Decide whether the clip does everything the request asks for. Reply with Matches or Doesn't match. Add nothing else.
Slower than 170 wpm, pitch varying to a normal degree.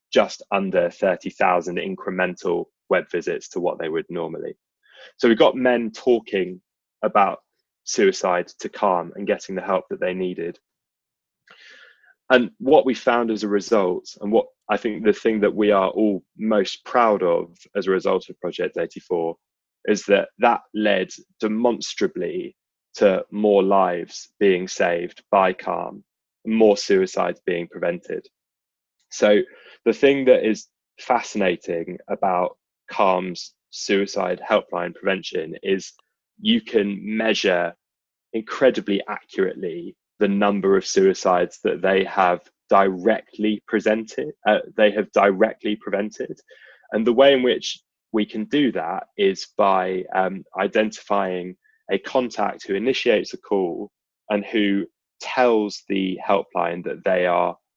Matches